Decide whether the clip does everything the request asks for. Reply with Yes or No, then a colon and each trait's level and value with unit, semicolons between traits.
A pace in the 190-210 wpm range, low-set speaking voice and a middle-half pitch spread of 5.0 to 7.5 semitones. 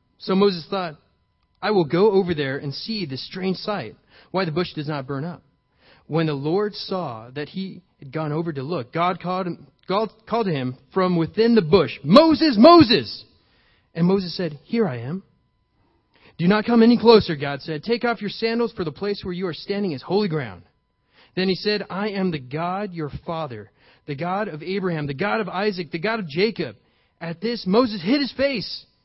No: average, 200 wpm; medium, 180 Hz; wide, 5.6 semitones